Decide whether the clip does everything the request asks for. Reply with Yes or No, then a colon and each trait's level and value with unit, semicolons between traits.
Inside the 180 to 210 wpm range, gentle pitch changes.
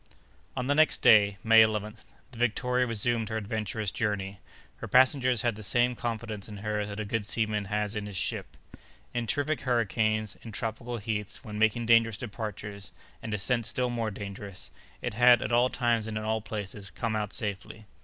Yes: average, 185 wpm; narrow, 2.2 semitones